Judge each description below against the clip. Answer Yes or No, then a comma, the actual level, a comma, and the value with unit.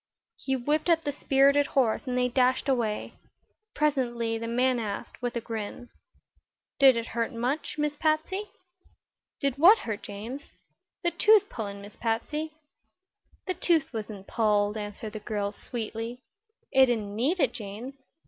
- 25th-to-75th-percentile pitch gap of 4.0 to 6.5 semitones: Yes, average, 4.5 semitones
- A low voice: No, high, 245 Hz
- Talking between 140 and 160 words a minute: Yes, average, 150 wpm